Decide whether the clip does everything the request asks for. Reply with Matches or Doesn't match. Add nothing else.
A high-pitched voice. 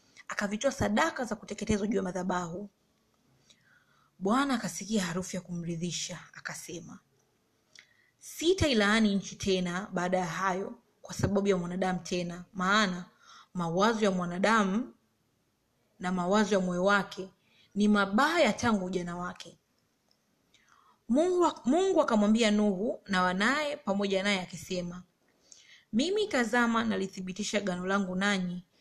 Matches